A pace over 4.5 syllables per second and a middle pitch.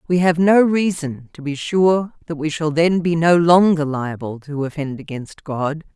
No: 4.3 syllables/s; medium, 160 Hz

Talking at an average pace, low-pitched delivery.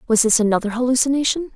No: average, 155 wpm; high, 245 Hz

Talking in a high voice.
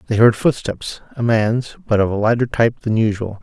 No: low, 110 Hz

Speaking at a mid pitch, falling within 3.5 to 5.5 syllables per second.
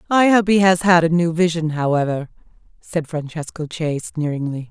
Yes: medium, 165 Hz; 5.3 syllables/s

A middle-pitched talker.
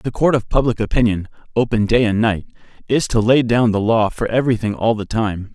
No: low, 110 Hz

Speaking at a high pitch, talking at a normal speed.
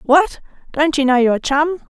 Yes: very high, 290 Hz; average, 185 wpm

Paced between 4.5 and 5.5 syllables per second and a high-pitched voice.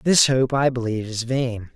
No: 5.0 syllables/s; low, 125 Hz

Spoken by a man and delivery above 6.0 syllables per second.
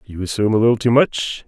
Yes: male; 6.6 syllables/s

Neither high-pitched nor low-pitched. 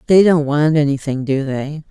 Yes: medium, 145 Hz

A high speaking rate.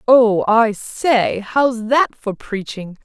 No: average, 140 wpm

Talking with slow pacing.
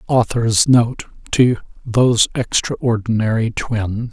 Yes: slow, 85 wpm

